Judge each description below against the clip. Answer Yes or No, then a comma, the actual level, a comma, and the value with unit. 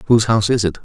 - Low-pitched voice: Yes, low, 110 Hz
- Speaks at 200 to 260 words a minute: No, fast, 285 wpm